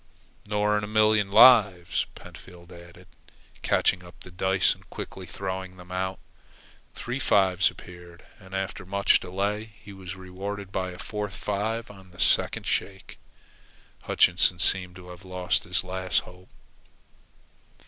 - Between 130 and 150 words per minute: Yes, average, 140 wpm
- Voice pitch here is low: Yes, very low, 95 Hz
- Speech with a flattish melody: Yes, narrow, 2.0 semitones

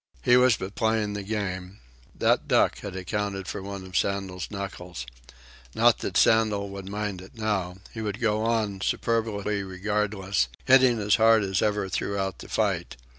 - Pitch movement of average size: No, narrow, 2.2 semitones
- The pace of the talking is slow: No, average, 165 wpm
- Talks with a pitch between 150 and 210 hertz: No, low, 100 Hz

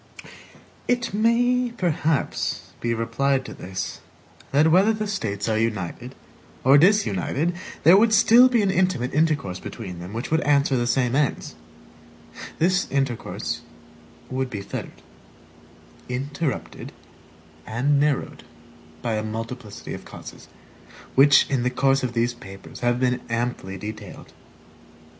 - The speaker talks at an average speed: No, slow, 130 wpm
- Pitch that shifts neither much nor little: No, wide, 6.0 semitones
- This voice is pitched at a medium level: No, low, 130 Hz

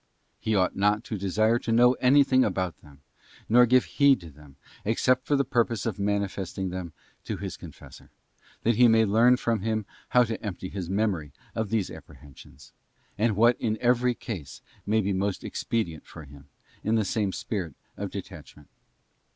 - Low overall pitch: Yes, low, 105 Hz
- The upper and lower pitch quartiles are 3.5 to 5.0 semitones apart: Yes, average, 4.1 semitones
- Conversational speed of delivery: Yes, average, 175 wpm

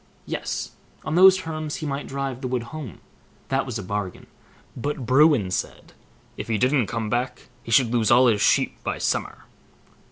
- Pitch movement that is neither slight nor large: Yes, average, 4.1 semitones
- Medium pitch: No, low, 130 Hz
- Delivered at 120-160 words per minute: No, average, 180 wpm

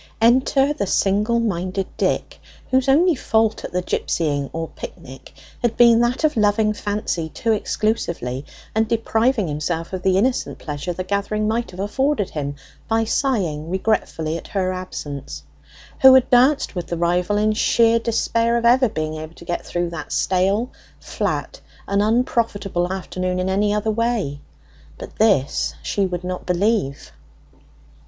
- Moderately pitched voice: No, high, 205 Hz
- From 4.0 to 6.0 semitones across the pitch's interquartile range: Yes, average, 4.9 semitones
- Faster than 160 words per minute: No, average, 155 wpm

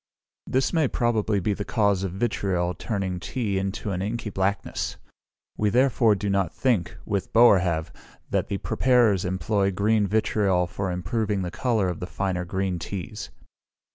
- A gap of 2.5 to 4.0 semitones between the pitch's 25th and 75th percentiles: Yes, average, 2.9 semitones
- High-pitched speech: No, low, 100 Hz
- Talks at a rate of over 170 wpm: No, average, 155 wpm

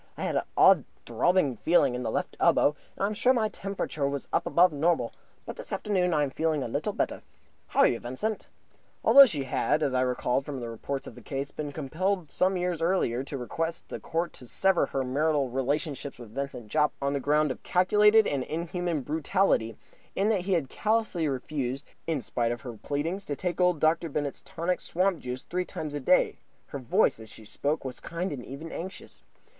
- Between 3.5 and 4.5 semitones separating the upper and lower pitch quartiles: No, average, 5.0 semitones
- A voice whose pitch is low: No, medium, 150 Hz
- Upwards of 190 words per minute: Yes, fast, 205 wpm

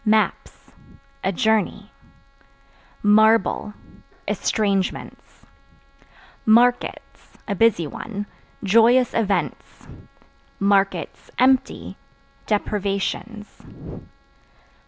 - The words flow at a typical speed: No, slow, 50 wpm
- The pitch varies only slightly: Yes, narrow, 2.1 semitones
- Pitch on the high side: Yes, high, 215 Hz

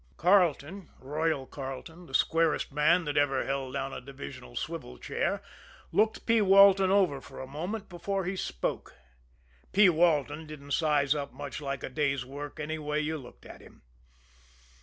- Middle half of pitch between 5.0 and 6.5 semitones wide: No, average, 4.2 semitones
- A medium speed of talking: Yes, average, 160 wpm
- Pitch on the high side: No, medium, 150 Hz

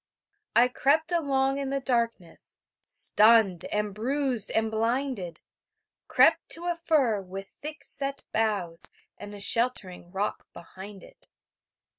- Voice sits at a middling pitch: No, high, 230 Hz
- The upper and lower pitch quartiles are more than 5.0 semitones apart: Yes, wide, 5.4 semitones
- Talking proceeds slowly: Yes, slow, 125 wpm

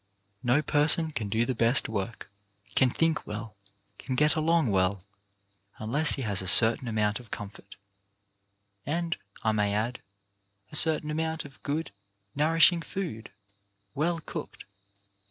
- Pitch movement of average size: No, wide, 6.4 semitones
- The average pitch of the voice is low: Yes, low, 130 Hz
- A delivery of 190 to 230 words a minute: No, average, 140 wpm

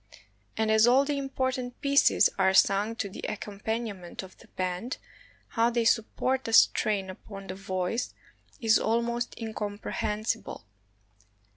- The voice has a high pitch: Yes, high, 220 Hz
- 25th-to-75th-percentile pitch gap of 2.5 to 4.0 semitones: Yes, average, 3.3 semitones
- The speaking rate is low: Yes, slow, 130 wpm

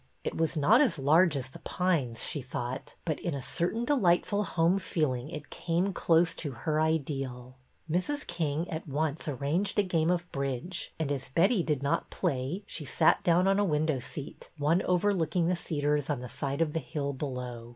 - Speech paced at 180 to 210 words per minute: Yes, average, 195 wpm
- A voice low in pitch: No, medium, 155 Hz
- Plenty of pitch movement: No, average, 4.0 semitones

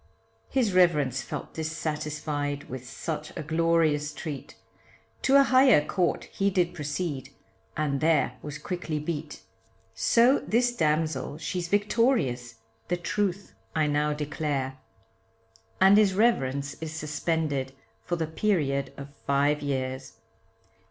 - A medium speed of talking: No, slow, 120 wpm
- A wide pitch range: No, average, 3.8 semitones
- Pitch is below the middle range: No, medium, 155 Hz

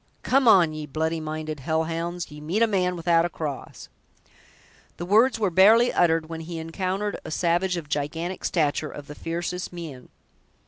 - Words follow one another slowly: No, average, 175 wpm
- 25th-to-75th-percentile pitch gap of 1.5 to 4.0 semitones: Yes, average, 2.7 semitones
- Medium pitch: Yes, medium, 165 Hz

